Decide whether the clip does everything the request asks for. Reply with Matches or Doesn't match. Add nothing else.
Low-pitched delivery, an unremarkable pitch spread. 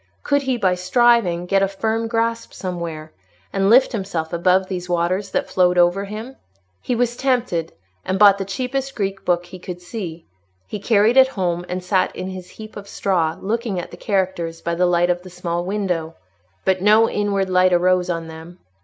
Doesn't match